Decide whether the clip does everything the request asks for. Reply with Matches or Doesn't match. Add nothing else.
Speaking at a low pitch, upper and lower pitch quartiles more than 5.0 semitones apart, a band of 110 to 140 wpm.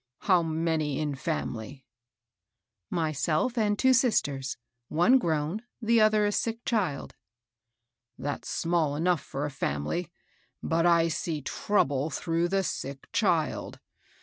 Doesn't match